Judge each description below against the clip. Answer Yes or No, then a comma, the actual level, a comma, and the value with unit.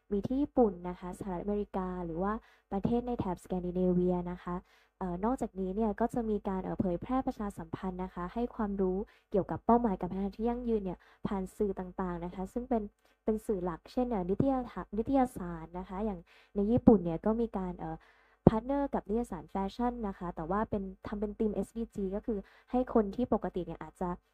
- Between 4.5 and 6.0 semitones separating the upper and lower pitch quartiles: No, average, 4.0 semitones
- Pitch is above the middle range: Yes, high, 200 Hz